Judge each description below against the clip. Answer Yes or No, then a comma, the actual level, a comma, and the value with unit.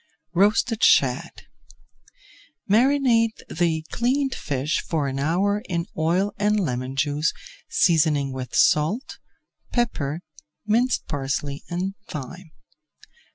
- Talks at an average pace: No, slow, 100 wpm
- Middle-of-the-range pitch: Yes, medium, 170 Hz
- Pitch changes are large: Yes, wide, 6.6 semitones